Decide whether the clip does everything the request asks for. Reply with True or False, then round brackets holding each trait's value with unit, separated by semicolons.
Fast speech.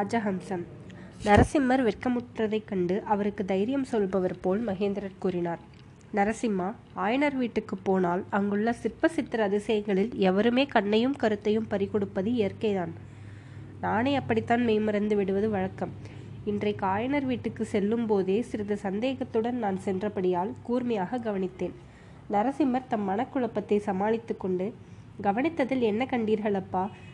False (100 wpm)